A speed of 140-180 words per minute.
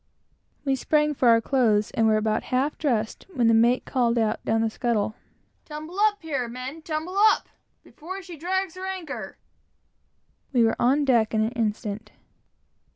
Yes: average, 170 wpm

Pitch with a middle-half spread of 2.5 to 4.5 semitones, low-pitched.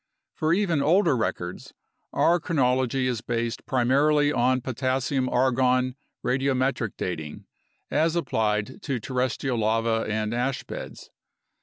Yes: average, 2.9 semitones; low, 130 Hz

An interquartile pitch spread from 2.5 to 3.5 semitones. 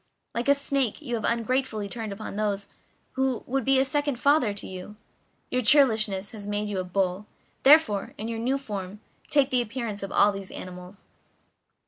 No: average, 4.6 semitones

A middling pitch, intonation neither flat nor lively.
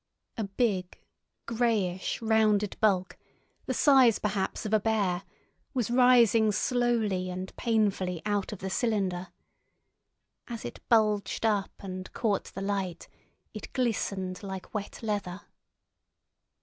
No: high, 205 Hz; average, 3.0 semitones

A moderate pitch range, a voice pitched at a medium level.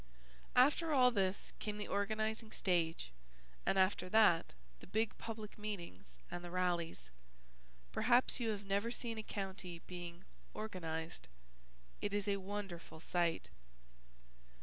No: average, 3.8 semitones; high, 195 Hz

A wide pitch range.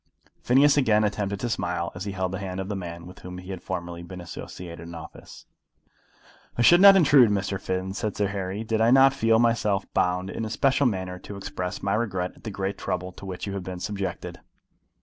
No: average, 3.3 semitones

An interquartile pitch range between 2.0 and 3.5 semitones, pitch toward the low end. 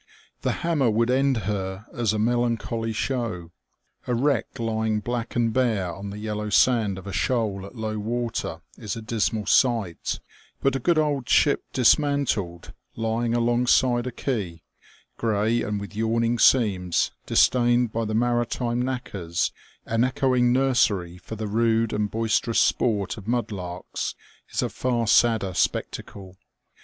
Yes: average, 2.7 semitones; low, 115 Hz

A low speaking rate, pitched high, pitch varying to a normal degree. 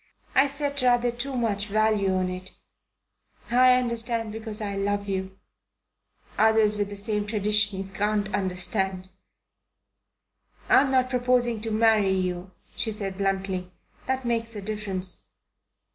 Yes: slow, 130 wpm; high, 210 Hz; average, 3.3 semitones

